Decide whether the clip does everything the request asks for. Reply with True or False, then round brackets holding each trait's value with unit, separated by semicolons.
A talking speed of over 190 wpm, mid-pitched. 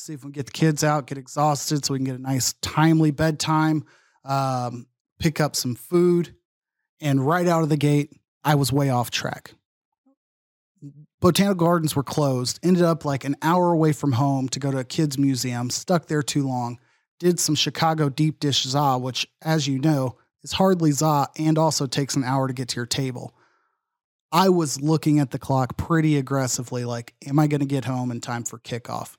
True (200 wpm; 145 Hz)